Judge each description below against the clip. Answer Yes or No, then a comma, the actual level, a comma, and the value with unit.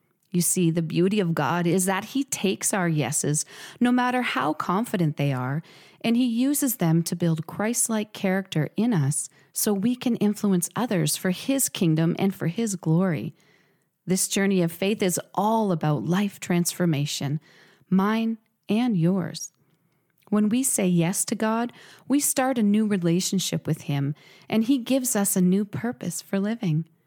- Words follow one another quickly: No, average, 165 wpm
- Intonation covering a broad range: No, average, 4.6 semitones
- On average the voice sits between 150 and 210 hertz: Yes, medium, 185 Hz